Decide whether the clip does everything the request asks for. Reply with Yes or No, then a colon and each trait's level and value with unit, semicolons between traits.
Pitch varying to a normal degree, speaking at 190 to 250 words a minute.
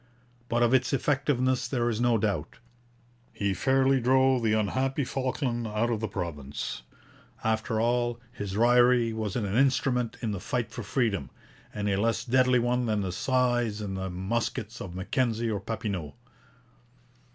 No: average, 3.4 semitones; average, 150 wpm